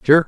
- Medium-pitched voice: Yes, medium, 155 Hz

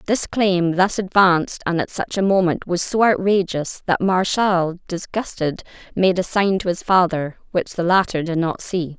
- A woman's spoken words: Yes, female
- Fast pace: No, average, 180 wpm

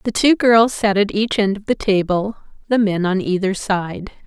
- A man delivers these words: No, female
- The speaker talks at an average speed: No, fast, 210 wpm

